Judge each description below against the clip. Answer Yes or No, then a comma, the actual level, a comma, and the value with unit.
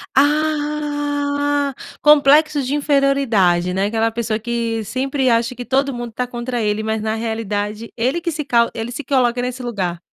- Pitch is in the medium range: No, high, 245 Hz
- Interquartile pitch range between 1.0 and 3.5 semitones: No, average, 4.2 semitones